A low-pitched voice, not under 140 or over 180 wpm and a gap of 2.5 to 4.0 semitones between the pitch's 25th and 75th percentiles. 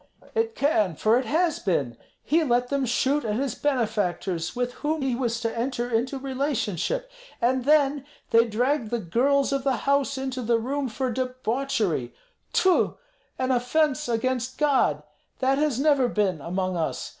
No: very high, 255 Hz; average, 160 wpm; average, 3.6 semitones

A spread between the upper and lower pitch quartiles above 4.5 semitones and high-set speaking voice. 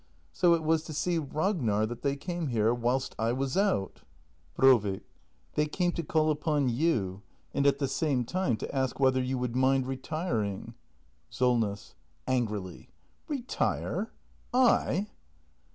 No: average, 4.9 semitones; low, 135 Hz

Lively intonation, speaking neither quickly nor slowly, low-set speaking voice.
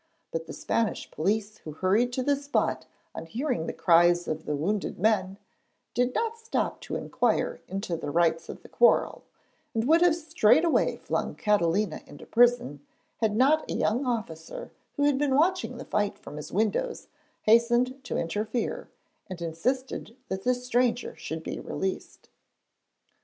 No: wide, 7.0 semitones; average, 160 wpm; high, 225 Hz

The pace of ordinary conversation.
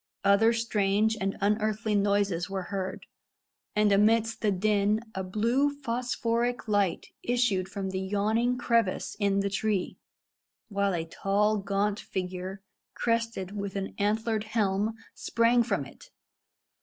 No: slow, 130 wpm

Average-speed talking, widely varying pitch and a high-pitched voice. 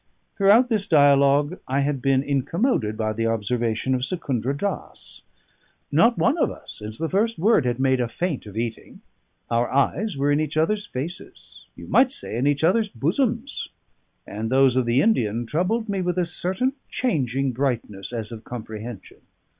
No: average, 170 wpm; wide, 7.7 semitones; medium, 140 Hz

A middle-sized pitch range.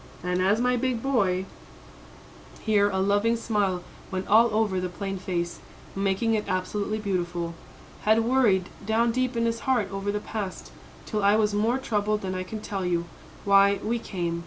Yes: average, 3.1 semitones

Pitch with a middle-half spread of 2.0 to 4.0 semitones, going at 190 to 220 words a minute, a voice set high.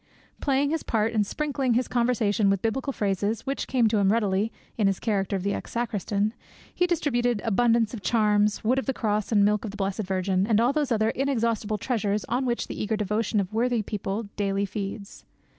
Yes: average, 3.1 semitones; fast, 205 wpm; high, 220 Hz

